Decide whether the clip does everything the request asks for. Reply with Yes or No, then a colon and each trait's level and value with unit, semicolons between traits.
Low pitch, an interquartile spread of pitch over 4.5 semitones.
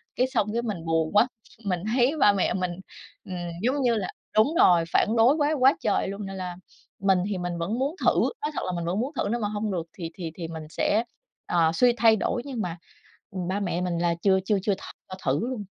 No: high, 195 Hz; average, 4.9 semitones